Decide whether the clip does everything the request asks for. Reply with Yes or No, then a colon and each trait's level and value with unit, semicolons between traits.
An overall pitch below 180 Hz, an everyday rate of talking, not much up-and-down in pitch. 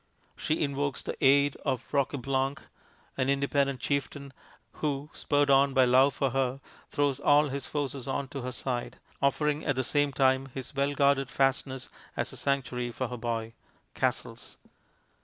Yes: low, 135 Hz; average, 160 wpm; narrow, 1.4 semitones